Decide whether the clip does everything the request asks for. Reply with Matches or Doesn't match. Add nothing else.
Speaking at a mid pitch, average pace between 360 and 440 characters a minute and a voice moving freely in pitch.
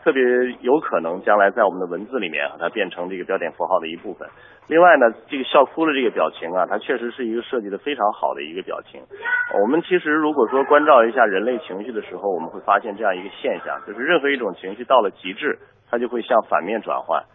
Matches